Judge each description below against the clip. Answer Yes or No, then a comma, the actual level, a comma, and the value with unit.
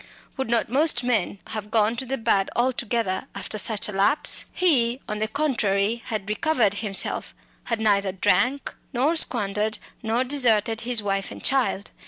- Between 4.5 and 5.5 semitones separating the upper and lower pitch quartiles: No, average, 3.5 semitones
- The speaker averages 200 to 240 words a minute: No, average, 160 wpm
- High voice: Yes, high, 225 Hz